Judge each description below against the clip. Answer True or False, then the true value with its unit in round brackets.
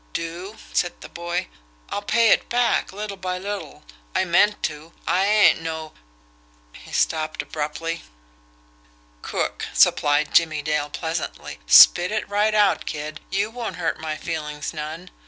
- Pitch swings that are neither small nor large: True (4.6 semitones)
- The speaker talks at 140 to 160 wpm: True (145 wpm)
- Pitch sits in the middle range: True (170 Hz)